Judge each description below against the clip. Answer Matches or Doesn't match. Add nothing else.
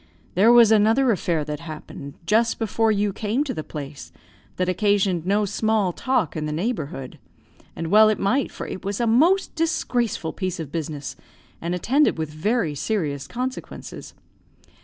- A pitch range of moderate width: Doesn't match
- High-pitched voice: Matches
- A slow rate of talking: Doesn't match